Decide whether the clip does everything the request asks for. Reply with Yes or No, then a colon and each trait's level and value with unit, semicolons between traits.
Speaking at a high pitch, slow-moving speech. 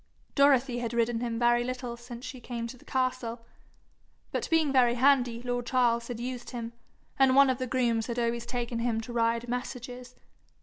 No: high, 245 Hz; average, 185 wpm